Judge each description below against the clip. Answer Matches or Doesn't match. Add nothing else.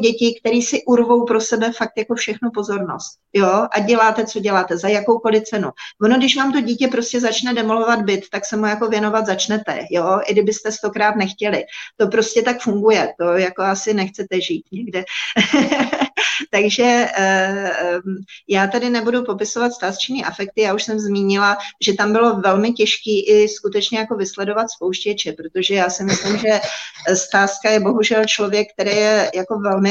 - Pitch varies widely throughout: Doesn't match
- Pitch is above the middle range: Matches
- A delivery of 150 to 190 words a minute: Matches